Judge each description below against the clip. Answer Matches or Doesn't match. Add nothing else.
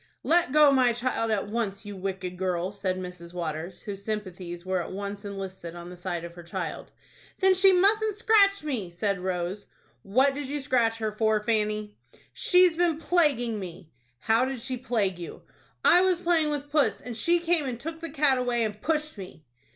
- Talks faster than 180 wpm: Matches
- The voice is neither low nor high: Doesn't match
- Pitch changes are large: Matches